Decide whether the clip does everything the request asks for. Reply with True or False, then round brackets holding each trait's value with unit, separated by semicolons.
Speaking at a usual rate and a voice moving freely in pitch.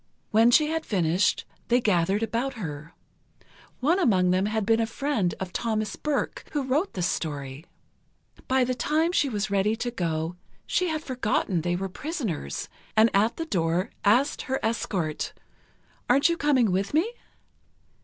True (160 wpm; 6.7 semitones)